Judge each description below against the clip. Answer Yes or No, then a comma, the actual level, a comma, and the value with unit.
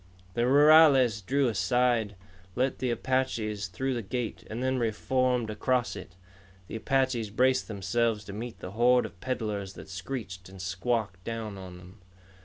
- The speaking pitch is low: Yes, low, 115 Hz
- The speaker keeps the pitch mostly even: No, average, 4.3 semitones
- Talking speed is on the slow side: No, average, 155 wpm